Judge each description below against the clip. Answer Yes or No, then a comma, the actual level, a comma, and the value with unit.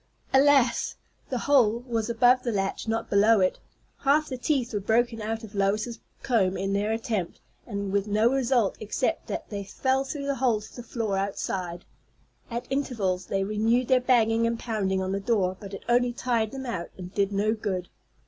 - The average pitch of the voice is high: Yes, high, 225 Hz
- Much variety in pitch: No, average, 3.6 semitones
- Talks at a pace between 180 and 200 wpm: Yes, average, 190 wpm